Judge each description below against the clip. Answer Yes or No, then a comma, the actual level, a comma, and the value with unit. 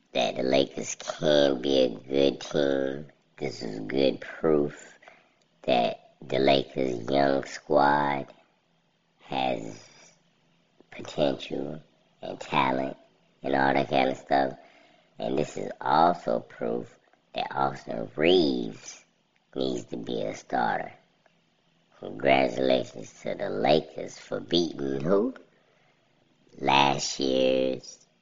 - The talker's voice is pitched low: Yes, very low, 70 Hz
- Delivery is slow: Yes, slow, 105 wpm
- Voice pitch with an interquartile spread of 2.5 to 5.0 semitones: No, narrow, 1.1 semitones